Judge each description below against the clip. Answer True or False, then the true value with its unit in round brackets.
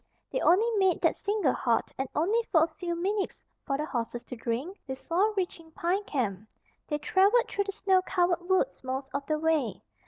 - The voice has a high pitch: True (335 Hz)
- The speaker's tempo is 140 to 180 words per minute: False (190 wpm)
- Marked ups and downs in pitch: True (6.1 semitones)